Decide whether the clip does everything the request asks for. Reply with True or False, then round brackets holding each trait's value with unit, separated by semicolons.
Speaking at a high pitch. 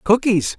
True (200 Hz)